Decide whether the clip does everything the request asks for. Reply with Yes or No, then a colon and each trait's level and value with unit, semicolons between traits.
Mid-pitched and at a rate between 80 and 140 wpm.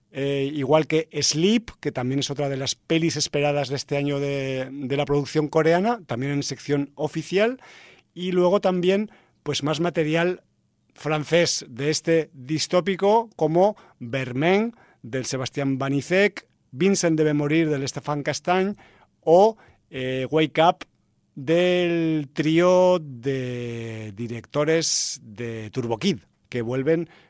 Yes: medium, 150 Hz; slow, 125 wpm